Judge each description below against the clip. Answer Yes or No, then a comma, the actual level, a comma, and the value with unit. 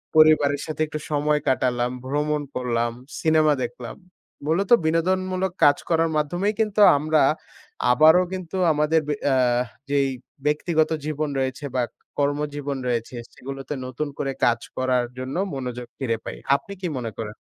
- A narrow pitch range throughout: No, average, 3.4 semitones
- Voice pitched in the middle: Yes, medium, 150 Hz